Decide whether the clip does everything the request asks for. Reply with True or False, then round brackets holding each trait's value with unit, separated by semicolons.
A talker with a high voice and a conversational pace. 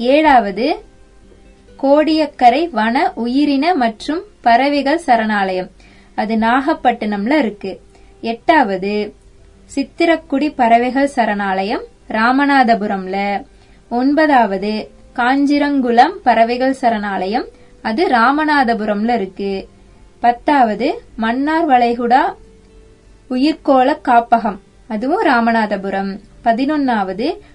False (240 Hz; 65 wpm)